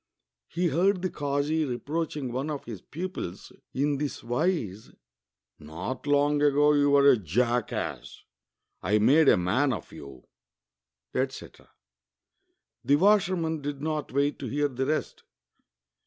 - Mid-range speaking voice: Yes, medium, 145 Hz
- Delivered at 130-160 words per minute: Yes, average, 140 wpm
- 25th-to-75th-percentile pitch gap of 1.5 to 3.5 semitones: No, average, 4.0 semitones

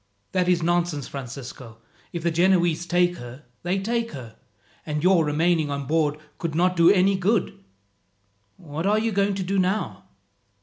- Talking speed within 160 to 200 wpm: Yes, average, 165 wpm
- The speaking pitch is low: No, medium, 175 Hz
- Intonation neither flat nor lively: Yes, average, 4.0 semitones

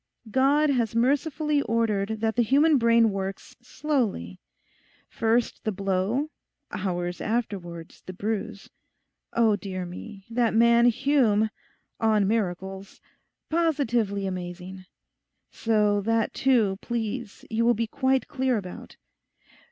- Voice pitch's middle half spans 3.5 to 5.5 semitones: Yes, average, 3.8 semitones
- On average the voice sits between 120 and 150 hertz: No, high, 225 Hz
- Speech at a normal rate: No, slow, 105 wpm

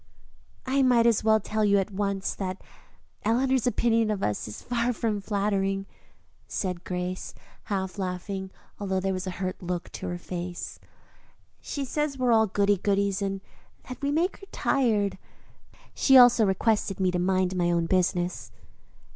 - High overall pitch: Yes, high, 200 Hz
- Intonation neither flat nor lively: Yes, average, 3.7 semitones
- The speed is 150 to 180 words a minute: Yes, average, 165 wpm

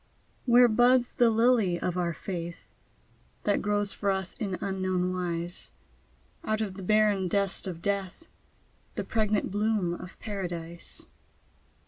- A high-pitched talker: Yes, high, 195 Hz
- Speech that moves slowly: Yes, slow, 130 wpm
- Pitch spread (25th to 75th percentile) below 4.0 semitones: Yes, average, 3.1 semitones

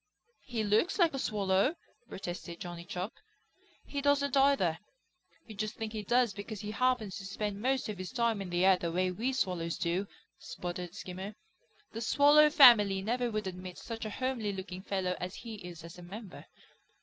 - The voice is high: Yes, high, 205 Hz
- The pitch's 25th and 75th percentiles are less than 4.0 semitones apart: No, average, 4.6 semitones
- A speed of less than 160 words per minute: No, average, 185 wpm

